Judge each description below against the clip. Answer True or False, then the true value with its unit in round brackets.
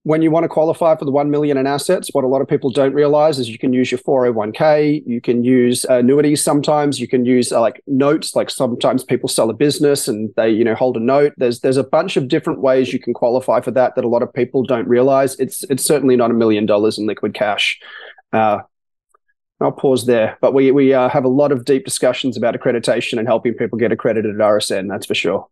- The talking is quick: True (240 wpm)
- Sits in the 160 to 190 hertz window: False (130 Hz)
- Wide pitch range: False (3.0 semitones)